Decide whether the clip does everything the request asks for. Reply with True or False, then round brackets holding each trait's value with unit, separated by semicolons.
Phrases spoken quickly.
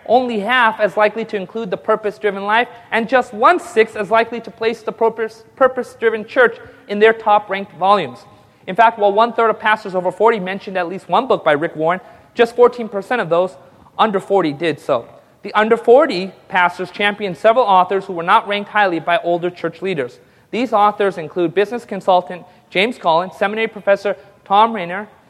False (185 wpm)